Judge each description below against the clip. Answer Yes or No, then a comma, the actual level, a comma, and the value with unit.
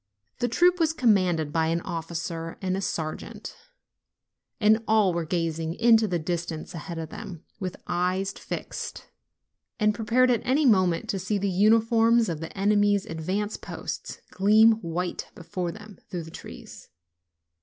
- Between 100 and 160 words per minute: Yes, average, 155 wpm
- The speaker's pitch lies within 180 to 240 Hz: Yes, high, 190 Hz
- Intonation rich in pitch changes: No, average, 4.5 semitones